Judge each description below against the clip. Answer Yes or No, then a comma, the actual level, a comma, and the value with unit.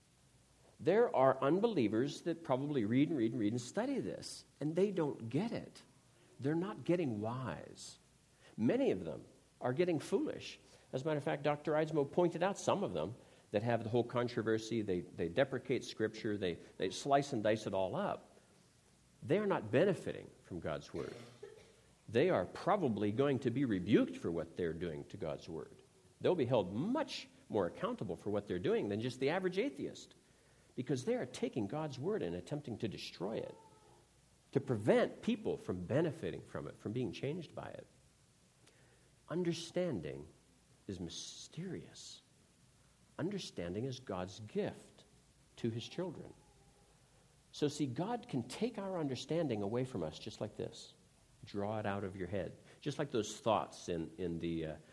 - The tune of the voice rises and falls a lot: Yes, wide, 7.5 semitones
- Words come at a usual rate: Yes, average, 165 wpm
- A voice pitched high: No, low, 135 Hz